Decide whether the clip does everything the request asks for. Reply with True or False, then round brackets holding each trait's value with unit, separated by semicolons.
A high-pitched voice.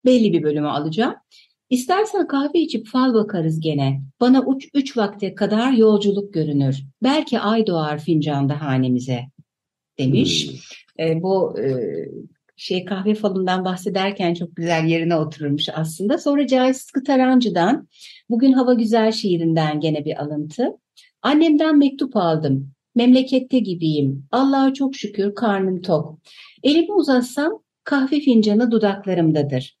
True (200 Hz)